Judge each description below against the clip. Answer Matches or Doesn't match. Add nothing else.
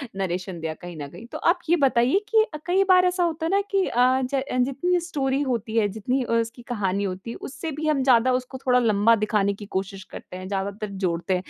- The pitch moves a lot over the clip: Matches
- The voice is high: Matches